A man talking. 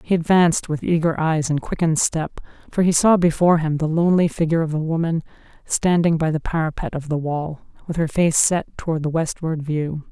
No: female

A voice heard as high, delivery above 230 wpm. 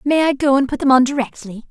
Yes: very high, 265 Hz; fast, 280 wpm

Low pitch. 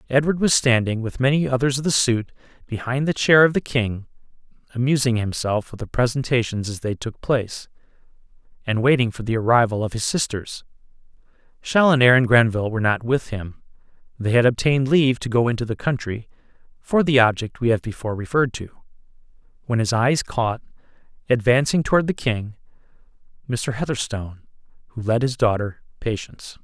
Yes: low, 120 Hz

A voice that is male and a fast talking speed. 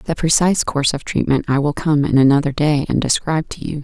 No: female; fast, 235 wpm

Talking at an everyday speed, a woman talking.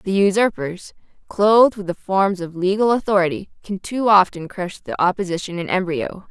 Yes: average, 160 wpm; female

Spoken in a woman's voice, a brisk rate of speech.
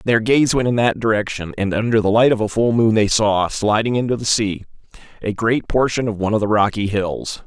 No: male; fast, 235 wpm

